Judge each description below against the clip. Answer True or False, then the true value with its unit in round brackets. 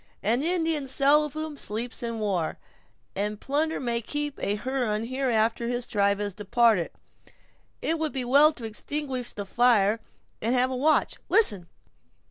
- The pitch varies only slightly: False (5.1 semitones)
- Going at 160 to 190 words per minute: False (145 wpm)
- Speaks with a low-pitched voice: False (245 Hz)